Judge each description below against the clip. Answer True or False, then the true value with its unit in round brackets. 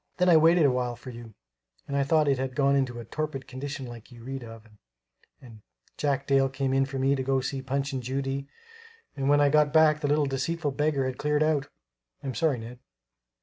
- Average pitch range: False (2.0 semitones)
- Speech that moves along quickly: True (230 wpm)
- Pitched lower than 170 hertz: True (135 Hz)